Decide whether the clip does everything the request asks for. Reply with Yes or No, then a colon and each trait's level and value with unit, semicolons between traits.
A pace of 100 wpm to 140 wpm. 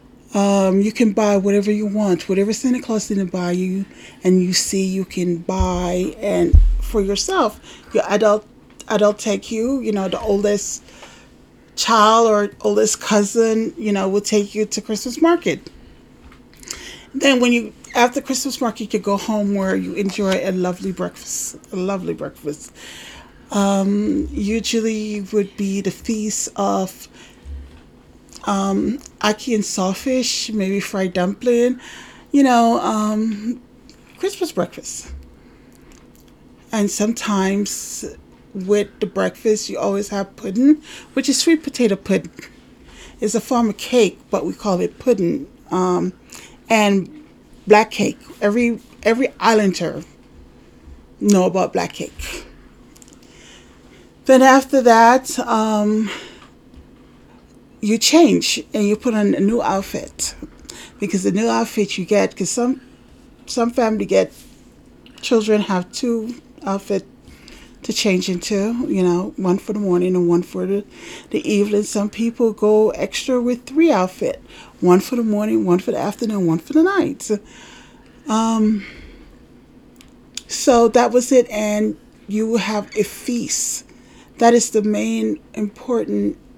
Yes: slow, 135 wpm